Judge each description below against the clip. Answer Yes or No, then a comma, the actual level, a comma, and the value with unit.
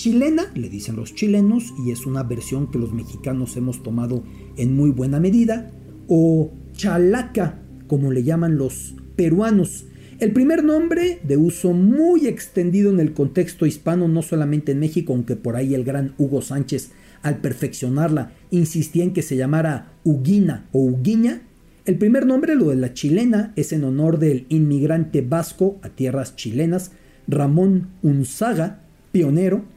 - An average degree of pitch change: No, wide, 6.2 semitones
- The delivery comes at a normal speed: Yes, average, 155 wpm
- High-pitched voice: No, medium, 160 Hz